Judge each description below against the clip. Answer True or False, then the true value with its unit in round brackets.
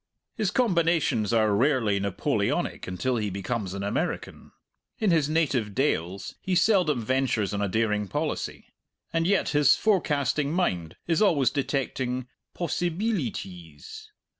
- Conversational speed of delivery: False (125 wpm)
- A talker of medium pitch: False (130 Hz)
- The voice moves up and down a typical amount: False (8.2 semitones)